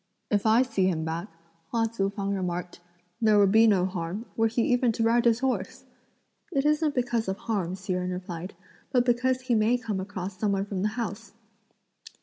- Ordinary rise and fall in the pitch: Yes, average, 3.9 semitones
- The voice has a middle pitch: No, high, 215 Hz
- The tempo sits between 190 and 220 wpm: Yes, average, 195 wpm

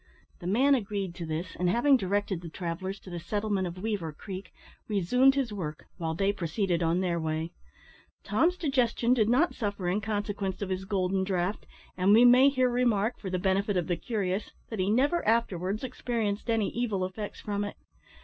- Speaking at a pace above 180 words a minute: Yes, average, 190 wpm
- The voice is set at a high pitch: Yes, high, 200 Hz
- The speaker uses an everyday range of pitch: Yes, average, 4.0 semitones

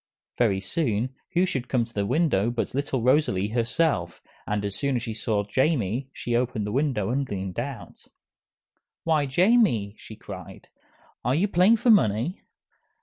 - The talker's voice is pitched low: Yes, low, 125 Hz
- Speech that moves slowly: No, average, 160 wpm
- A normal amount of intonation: No, wide, 6.0 semitones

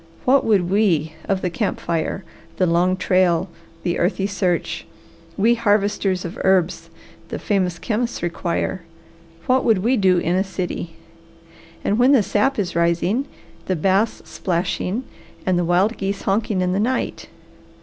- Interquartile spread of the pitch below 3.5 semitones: Yes, average, 3.0 semitones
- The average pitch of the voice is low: No, high, 190 Hz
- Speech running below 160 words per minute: Yes, average, 150 wpm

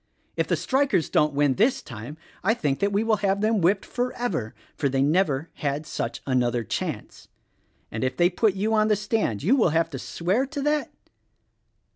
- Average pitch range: No, wide, 7.7 semitones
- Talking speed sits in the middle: Yes, average, 190 wpm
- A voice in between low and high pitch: Yes, medium, 180 Hz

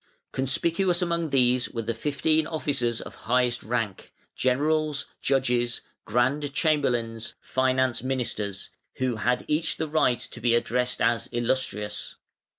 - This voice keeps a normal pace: No, slow, 125 wpm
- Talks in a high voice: No, low, 125 Hz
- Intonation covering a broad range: No, average, 3.7 semitones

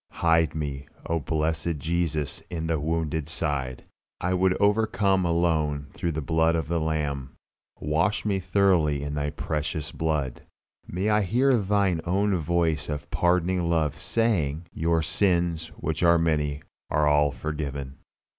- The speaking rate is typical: Yes, average, 145 wpm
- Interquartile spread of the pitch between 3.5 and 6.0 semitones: No, average, 3.0 semitones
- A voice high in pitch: No, very low, 80 Hz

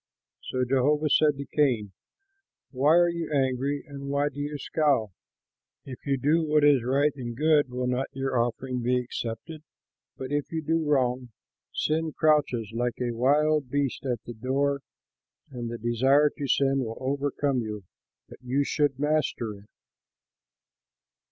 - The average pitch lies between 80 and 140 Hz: Yes, low, 135 Hz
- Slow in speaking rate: No, average, 155 wpm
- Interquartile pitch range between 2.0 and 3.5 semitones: Yes, average, 2.9 semitones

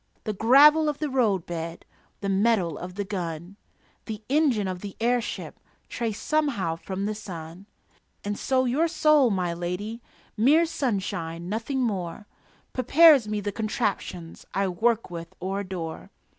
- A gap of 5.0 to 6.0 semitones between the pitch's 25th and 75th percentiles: Yes, wide, 5.6 semitones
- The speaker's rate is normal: Yes, average, 145 wpm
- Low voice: No, high, 205 Hz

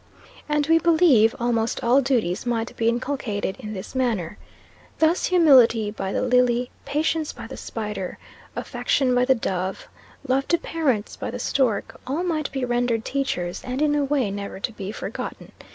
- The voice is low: No, high, 245 Hz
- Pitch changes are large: No, average, 4.6 semitones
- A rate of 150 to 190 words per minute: Yes, average, 170 wpm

